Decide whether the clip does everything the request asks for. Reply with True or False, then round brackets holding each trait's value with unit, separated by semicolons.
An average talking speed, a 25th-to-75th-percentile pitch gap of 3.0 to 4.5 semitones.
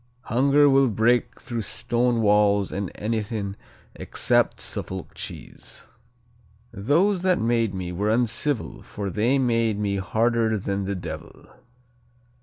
False (125 wpm; 3.4 semitones)